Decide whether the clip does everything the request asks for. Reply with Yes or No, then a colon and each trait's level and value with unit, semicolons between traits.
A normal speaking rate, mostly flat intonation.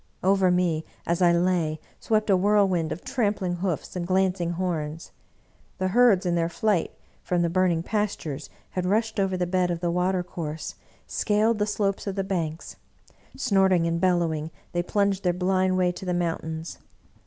Yes: average, 175 wpm; narrow, 2.2 semitones